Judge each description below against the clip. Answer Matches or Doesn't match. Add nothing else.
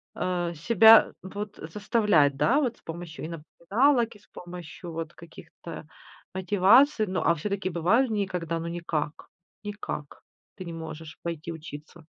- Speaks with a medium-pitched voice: Matches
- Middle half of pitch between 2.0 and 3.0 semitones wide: Doesn't match